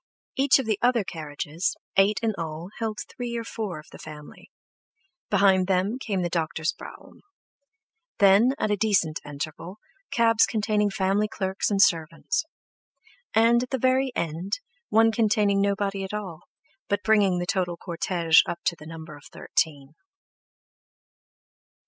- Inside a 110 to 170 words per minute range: Yes, average, 145 wpm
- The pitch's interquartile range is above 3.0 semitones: Yes, average, 4.5 semitones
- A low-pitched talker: No, high, 195 Hz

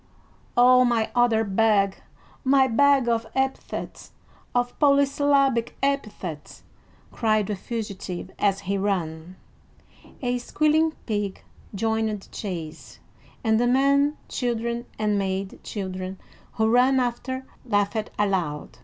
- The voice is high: Yes, high, 225 Hz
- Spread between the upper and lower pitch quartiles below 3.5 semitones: No, average, 4.4 semitones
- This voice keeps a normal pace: No, slow, 110 wpm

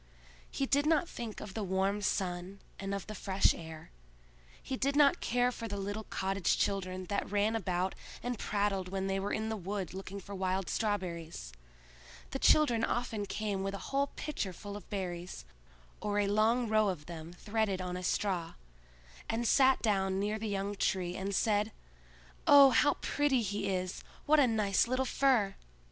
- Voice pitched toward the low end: No, high, 200 Hz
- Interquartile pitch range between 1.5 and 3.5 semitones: Yes, average, 3.0 semitones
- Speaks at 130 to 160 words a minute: No, average, 180 wpm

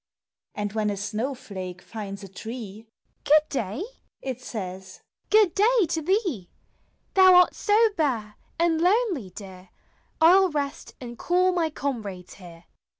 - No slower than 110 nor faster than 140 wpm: No, average, 150 wpm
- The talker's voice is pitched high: Yes, very high, 250 Hz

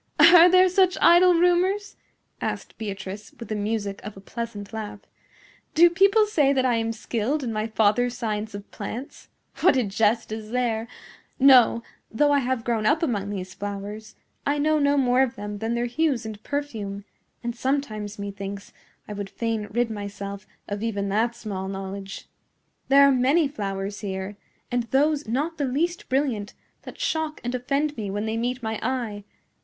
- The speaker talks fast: No, average, 175 wpm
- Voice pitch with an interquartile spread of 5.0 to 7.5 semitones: Yes, average, 5.3 semitones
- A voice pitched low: No, high, 230 Hz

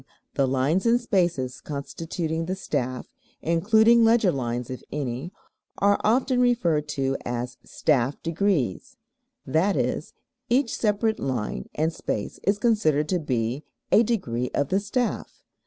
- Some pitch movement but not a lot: No, wide, 8.0 semitones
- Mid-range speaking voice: Yes, medium, 165 Hz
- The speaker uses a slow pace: Yes, slow, 130 wpm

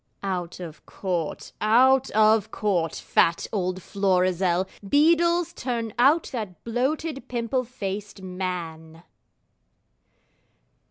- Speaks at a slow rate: Yes, slow, 95 wpm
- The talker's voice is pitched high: Yes, high, 205 Hz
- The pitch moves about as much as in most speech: No, wide, 5.7 semitones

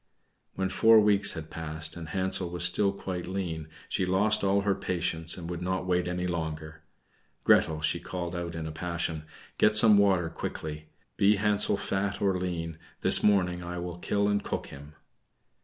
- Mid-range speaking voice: No, very low, 90 Hz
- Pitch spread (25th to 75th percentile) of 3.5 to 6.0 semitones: No, average, 3.1 semitones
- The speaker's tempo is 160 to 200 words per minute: Yes, average, 175 wpm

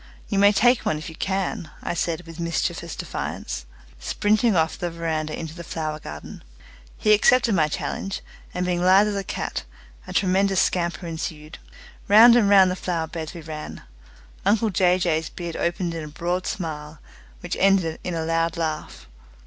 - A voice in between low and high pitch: Yes, medium, 175 Hz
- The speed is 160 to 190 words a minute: Yes, average, 175 wpm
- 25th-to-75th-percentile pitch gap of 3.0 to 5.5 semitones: Yes, average, 3.4 semitones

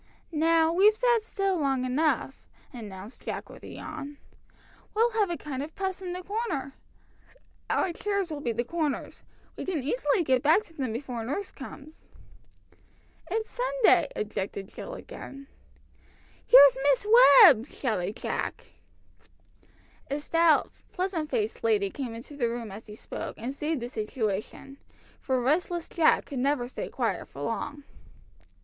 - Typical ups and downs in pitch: No, wide, 6.7 semitones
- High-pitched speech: Yes, very high, 290 Hz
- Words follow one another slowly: No, average, 150 wpm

